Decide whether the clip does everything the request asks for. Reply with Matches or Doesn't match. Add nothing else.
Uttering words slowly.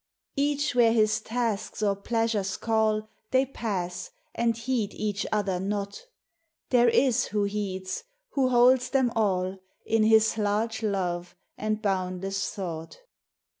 Matches